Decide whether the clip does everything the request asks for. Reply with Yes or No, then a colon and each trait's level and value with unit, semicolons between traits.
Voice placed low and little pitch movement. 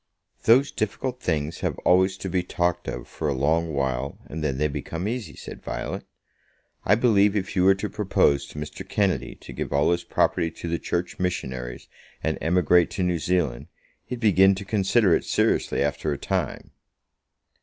No: very low, 90 Hz; average, 4.6 semitones